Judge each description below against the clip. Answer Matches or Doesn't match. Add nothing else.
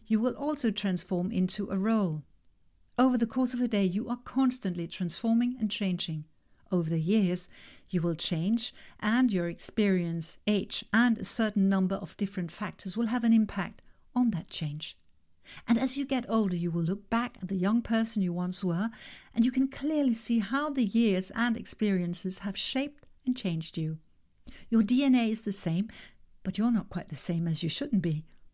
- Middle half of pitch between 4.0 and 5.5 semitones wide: Matches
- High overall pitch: Matches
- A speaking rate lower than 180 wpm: Doesn't match